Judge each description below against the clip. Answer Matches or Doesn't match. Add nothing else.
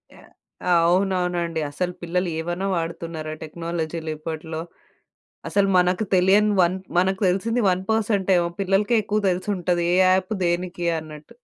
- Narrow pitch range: Matches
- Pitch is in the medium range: Matches